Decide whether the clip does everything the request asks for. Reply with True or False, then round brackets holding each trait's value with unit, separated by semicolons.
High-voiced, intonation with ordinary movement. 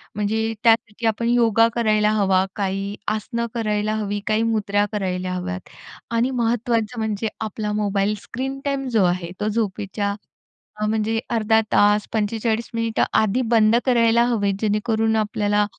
False (215 Hz; 1.8 semitones)